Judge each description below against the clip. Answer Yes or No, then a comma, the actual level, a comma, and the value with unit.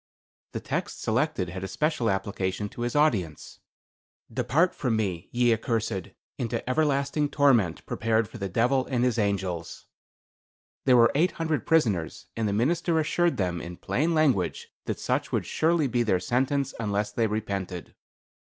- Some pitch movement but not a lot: No, wide, 6.2 semitones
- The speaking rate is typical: Yes, average, 155 wpm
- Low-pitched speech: Yes, low, 115 Hz